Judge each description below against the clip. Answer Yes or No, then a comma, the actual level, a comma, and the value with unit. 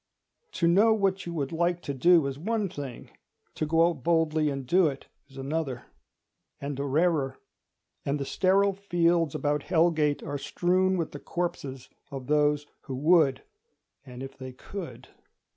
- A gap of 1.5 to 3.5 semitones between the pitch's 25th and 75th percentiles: No, average, 4.1 semitones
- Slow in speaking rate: No, average, 160 wpm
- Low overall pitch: No, medium, 155 Hz